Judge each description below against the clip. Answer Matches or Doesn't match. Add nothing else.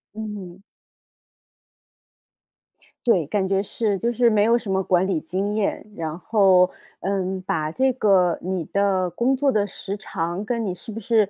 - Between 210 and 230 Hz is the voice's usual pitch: Doesn't match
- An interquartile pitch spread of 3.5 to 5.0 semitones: Doesn't match